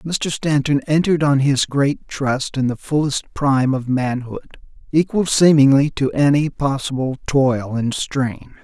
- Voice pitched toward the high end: No, medium, 140 Hz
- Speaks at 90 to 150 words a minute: Yes, average, 145 wpm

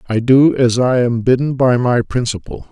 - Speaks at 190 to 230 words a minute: Yes, average, 200 wpm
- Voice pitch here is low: Yes, low, 125 Hz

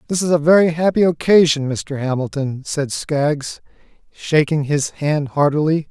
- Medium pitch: Yes, medium, 150 Hz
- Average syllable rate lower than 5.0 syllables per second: Yes, 4.4 syllables/s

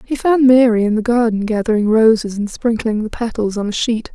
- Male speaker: No, female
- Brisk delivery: Yes, fast, 215 wpm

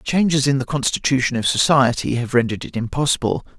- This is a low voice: Yes, low, 130 Hz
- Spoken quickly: No, average, 165 wpm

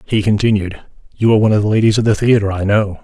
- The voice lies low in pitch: Yes, low, 105 Hz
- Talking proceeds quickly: Yes, fast, 255 wpm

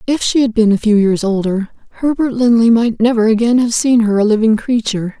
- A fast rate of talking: Yes, fast, 220 wpm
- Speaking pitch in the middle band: No, high, 225 Hz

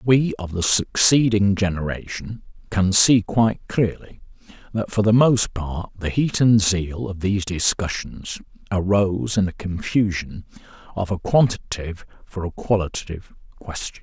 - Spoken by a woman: No, male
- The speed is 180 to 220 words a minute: No, slow, 135 wpm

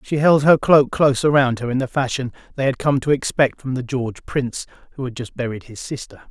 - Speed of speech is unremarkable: No, fast, 240 wpm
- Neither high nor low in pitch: No, low, 130 Hz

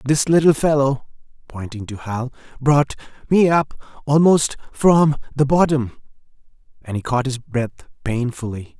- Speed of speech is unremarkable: No, slow, 90 wpm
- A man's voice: Yes, male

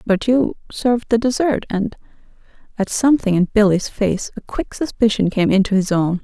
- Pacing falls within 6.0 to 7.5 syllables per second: No, 5.2 syllables/s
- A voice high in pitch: Yes, high, 215 Hz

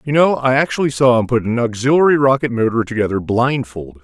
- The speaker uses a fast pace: No, average, 195 wpm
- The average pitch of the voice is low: Yes, low, 125 Hz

